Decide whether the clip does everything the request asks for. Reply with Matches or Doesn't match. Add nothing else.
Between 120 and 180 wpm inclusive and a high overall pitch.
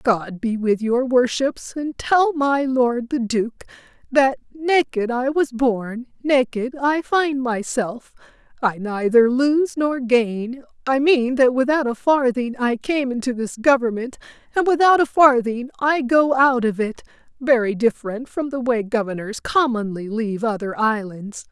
Matches